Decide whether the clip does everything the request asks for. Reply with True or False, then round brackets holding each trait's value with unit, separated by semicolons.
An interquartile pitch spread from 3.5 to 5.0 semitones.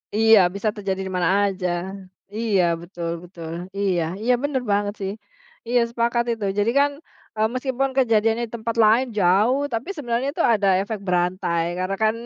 True (3.8 semitones)